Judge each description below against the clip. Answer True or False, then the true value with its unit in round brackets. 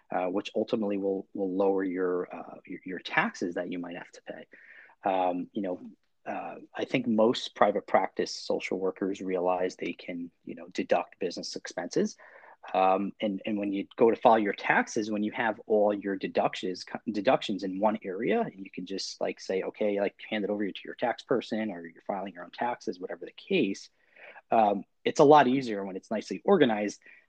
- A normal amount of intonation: False (2.1 semitones)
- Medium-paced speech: True (195 wpm)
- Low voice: True (100 Hz)